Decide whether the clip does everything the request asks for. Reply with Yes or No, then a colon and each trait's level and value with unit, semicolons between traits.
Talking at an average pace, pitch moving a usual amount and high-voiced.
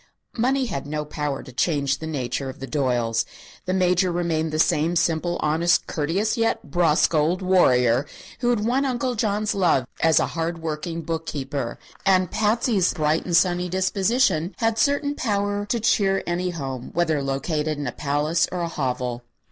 No: average, 170 wpm; average, 4.7 semitones; medium, 165 Hz